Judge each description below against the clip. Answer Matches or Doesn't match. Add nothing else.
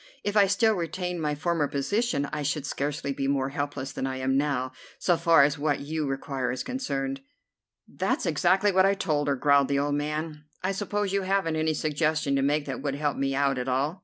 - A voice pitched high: Doesn't match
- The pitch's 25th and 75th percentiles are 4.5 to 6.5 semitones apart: Doesn't match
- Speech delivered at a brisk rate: Matches